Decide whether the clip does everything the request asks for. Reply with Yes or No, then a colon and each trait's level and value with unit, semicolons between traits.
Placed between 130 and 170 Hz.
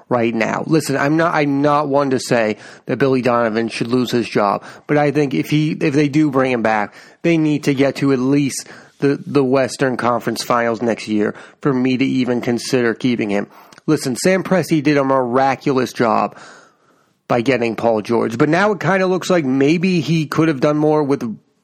Yes: low, 135 Hz